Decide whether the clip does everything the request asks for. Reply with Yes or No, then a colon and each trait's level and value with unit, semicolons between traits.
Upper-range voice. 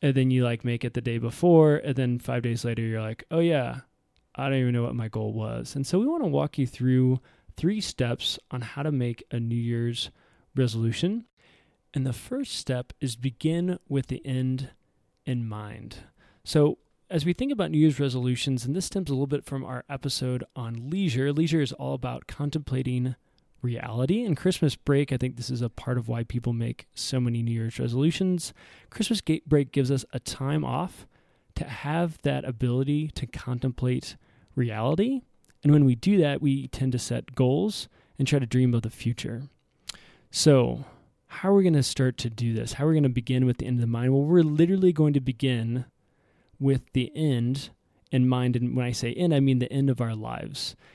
No: low, 130 Hz